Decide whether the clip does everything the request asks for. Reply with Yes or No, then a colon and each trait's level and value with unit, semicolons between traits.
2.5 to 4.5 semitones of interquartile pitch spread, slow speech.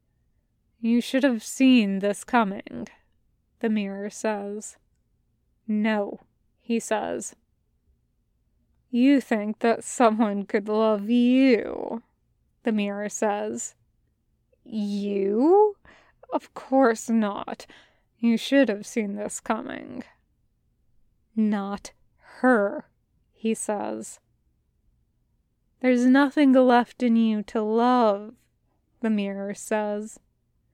Yes: average, 2.9 semitones; slow, 90 wpm